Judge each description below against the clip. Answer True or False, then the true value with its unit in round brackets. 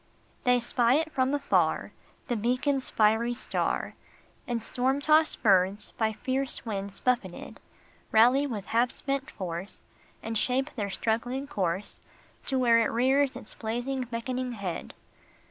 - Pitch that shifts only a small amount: False (3.4 semitones)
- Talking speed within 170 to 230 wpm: False (140 wpm)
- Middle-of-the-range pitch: False (240 Hz)